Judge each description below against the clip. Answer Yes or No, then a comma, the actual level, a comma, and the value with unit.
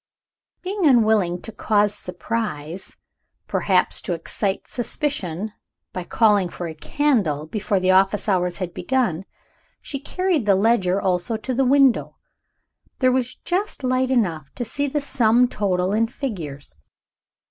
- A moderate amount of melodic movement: No, wide, 6.0 semitones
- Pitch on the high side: Yes, high, 210 Hz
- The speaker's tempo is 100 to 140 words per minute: Yes, slow, 135 wpm